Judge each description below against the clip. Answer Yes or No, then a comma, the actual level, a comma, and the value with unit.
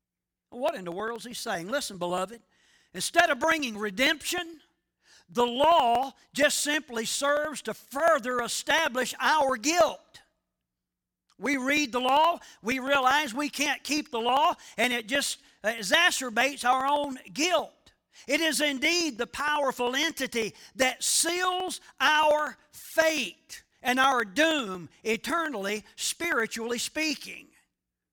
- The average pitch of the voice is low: No, very high, 270 Hz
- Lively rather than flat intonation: No, average, 4.6 semitones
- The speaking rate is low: Yes, slow, 120 wpm